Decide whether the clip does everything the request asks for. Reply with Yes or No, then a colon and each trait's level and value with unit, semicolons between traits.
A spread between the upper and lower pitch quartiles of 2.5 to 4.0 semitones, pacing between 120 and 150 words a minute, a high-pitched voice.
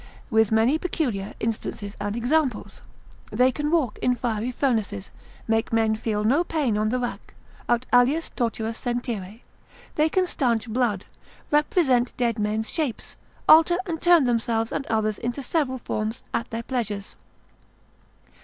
Yes: average, 3.7 semitones; average, 145 wpm; high, 240 Hz